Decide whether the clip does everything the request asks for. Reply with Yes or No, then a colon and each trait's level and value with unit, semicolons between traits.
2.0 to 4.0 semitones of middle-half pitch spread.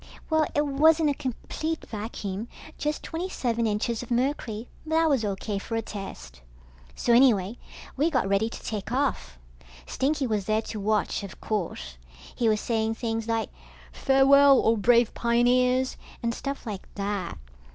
No: average, 4.4 semitones